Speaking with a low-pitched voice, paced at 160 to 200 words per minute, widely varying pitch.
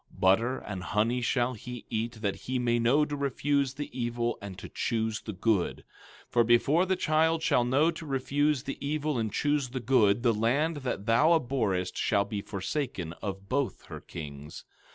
No: low, 120 Hz; average, 190 wpm; average, 5.0 semitones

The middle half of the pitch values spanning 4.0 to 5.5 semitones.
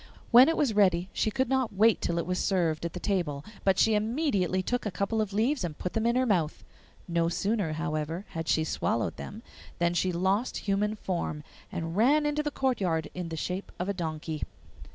Yes: average, 4.8 semitones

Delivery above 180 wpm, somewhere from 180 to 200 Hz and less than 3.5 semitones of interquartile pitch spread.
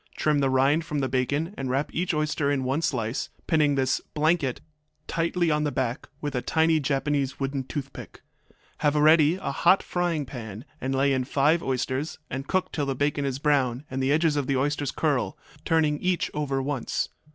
No: average, 190 wpm; medium, 145 Hz; narrow, 2.5 semitones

